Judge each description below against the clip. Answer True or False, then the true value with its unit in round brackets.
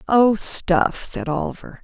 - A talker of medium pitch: True (180 Hz)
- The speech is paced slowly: True (130 wpm)